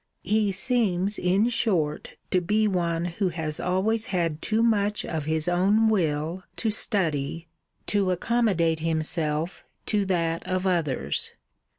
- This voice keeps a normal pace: No, slow, 130 wpm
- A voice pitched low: No, medium, 180 Hz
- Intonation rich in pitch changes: No, average, 4.2 semitones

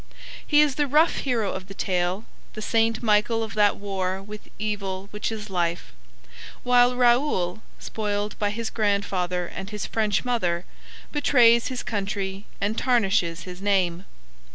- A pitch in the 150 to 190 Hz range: No, high, 210 Hz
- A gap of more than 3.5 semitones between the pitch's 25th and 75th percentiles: No, average, 3.2 semitones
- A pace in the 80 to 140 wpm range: No, average, 150 wpm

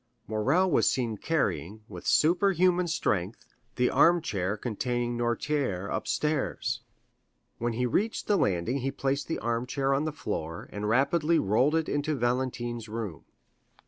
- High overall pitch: No, low, 125 Hz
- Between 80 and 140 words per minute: Yes, slow, 135 wpm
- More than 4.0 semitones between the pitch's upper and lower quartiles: Yes, wide, 5.6 semitones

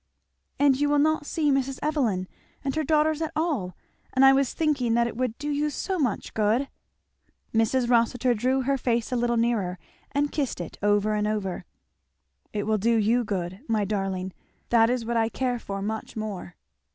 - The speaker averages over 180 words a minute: Yes, average, 190 wpm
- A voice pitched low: No, high, 235 Hz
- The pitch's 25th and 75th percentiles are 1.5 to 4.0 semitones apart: No, average, 4.6 semitones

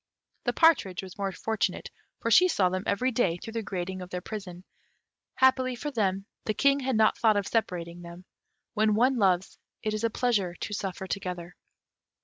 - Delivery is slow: No, average, 185 wpm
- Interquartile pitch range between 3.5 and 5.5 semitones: Yes, average, 4.0 semitones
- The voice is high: Yes, high, 200 Hz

